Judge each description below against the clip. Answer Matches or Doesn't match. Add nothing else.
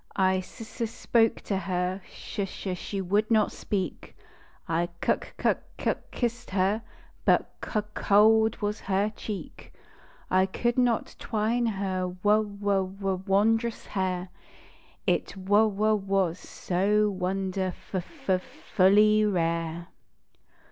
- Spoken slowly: Matches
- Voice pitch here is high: Matches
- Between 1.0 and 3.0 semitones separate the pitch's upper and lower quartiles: Matches